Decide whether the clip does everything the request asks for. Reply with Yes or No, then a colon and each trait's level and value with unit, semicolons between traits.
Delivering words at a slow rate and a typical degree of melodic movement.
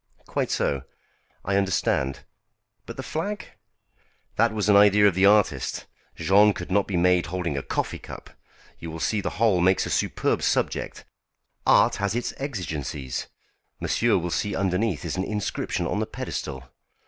No: average, 160 wpm; average, 3.3 semitones